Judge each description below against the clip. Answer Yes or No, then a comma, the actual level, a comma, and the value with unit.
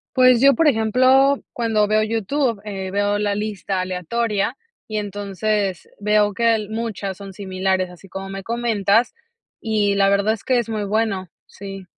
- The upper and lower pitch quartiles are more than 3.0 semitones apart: No, narrow, 2.6 semitones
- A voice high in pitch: Yes, high, 210 Hz